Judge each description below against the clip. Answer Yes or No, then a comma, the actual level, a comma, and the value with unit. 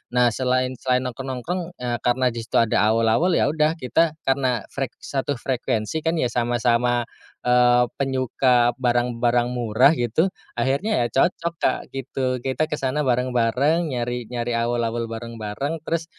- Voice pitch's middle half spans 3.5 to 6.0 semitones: No, narrow, 2.4 semitones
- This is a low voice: Yes, low, 125 Hz